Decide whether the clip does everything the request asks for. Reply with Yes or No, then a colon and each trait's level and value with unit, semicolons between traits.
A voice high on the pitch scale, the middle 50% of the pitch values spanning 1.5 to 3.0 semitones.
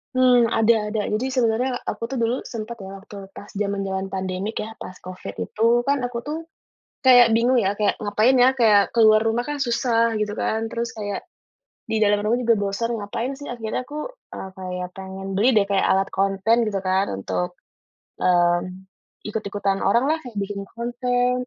No: high, 220 Hz; average, 3.6 semitones